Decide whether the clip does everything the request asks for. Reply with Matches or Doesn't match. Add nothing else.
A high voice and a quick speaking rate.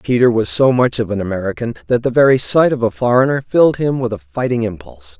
Doesn't match